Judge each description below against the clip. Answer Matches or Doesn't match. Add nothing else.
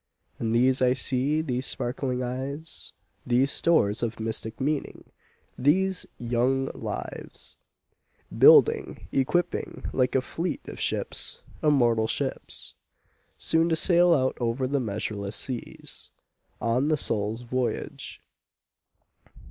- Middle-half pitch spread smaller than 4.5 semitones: Matches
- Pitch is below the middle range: Matches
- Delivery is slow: Matches